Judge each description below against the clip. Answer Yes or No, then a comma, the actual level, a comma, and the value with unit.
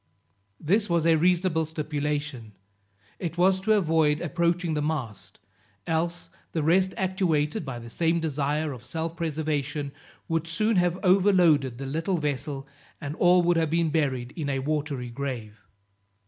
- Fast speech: No, average, 145 wpm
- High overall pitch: No, medium, 160 Hz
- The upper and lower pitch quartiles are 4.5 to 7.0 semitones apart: No, average, 3.1 semitones